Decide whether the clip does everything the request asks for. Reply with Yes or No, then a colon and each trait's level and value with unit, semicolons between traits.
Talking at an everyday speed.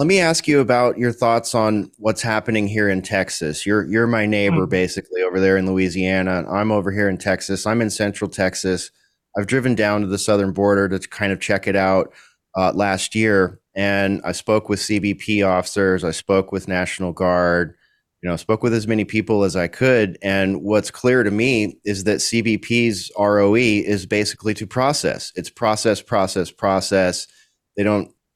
Yes: average, 185 wpm